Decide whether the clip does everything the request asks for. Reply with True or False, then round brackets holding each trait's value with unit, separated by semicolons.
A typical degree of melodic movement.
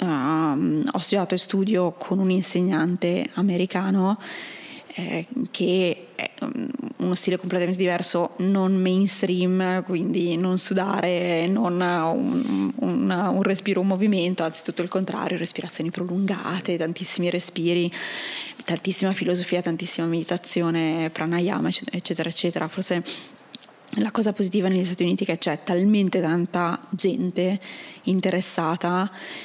False (1.8 semitones)